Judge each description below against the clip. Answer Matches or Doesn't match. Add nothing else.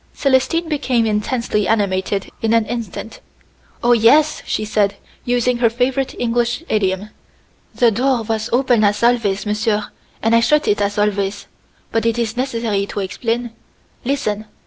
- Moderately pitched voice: Doesn't match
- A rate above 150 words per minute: Doesn't match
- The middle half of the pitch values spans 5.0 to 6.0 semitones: Doesn't match